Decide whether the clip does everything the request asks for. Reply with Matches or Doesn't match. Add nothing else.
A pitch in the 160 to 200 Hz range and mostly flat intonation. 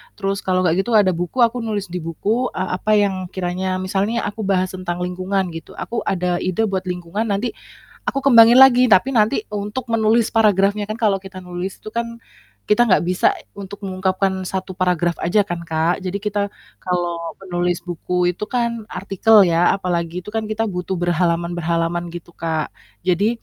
Doesn't match